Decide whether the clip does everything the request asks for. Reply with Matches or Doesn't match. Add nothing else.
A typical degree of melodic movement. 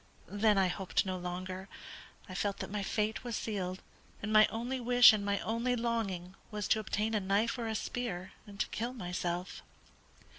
Matches